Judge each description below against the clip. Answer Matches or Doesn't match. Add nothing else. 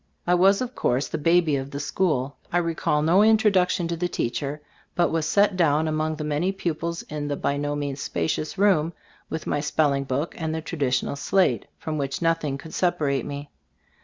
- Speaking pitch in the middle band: Matches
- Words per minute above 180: Matches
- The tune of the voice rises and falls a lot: Doesn't match